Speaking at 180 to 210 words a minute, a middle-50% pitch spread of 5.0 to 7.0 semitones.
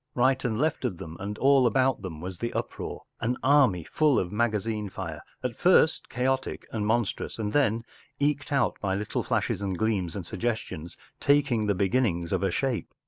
Yes: average, 190 wpm; average, 5.3 semitones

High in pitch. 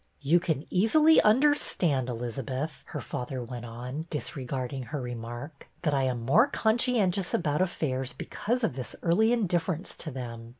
No: medium, 145 Hz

